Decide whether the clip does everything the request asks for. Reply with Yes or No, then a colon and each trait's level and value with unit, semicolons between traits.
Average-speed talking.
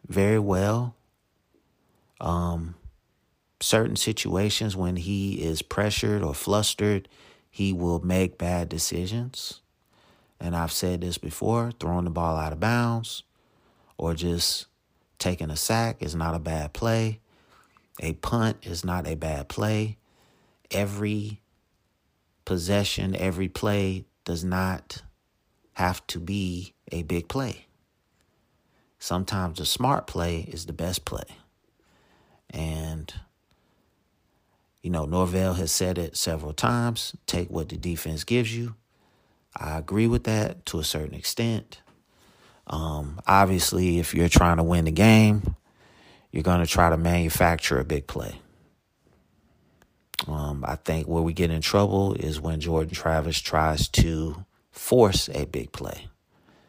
No: slow, 130 wpm